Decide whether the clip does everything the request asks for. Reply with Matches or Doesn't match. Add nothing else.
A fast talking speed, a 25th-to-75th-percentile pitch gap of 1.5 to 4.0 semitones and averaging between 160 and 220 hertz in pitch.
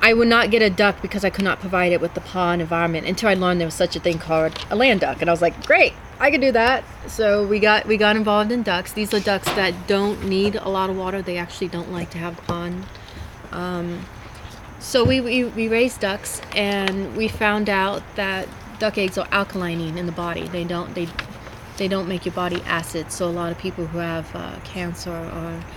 Matches